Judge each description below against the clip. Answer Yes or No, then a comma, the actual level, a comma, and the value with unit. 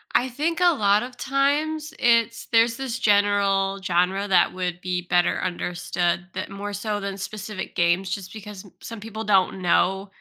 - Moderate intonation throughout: Yes, average, 3.7 semitones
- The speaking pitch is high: Yes, high, 205 Hz